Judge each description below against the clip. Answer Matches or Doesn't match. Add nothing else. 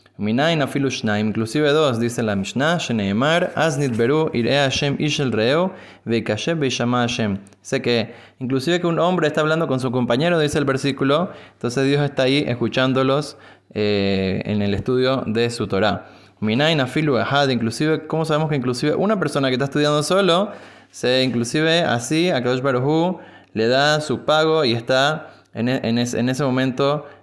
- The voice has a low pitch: Matches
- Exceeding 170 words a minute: Doesn't match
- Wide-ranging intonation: Doesn't match